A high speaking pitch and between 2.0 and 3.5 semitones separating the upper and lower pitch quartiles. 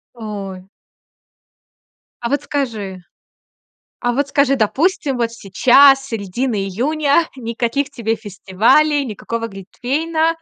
No: high, 245 Hz; average, 4.9 semitones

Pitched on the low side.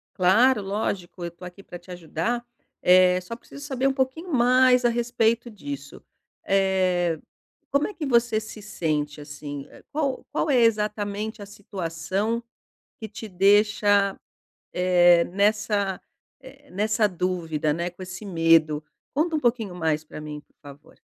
No: high, 200 Hz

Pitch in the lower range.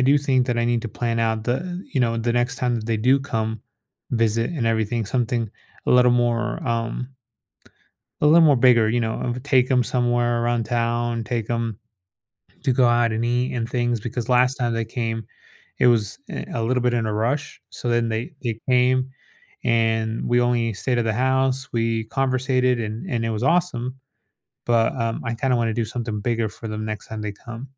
Yes: low, 120 Hz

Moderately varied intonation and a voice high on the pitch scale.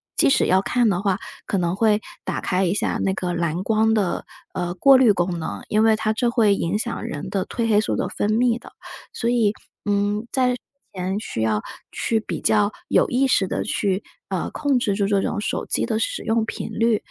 Yes: average, 3.2 semitones; high, 210 Hz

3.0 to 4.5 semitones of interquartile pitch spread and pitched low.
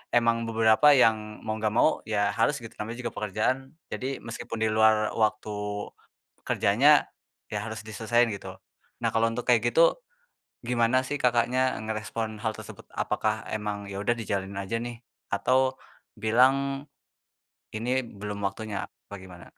No: narrow, 2.5 semitones; low, 110 Hz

